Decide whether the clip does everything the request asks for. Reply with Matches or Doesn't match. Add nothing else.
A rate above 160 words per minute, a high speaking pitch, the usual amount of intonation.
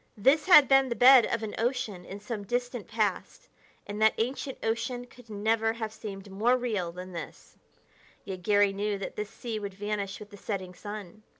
Matches